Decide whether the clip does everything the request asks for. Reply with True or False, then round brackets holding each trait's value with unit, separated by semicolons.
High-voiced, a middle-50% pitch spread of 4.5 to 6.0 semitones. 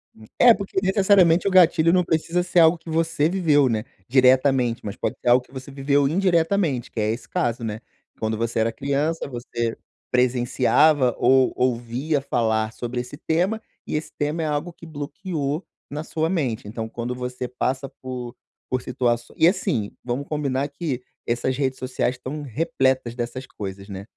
False (135 Hz; 4.9 semitones)